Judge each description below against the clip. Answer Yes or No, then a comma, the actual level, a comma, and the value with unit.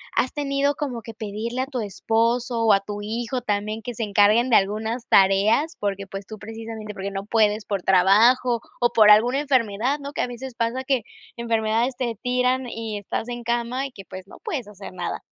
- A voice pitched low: No, high, 230 Hz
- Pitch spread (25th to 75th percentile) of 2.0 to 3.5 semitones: Yes, average, 3.1 semitones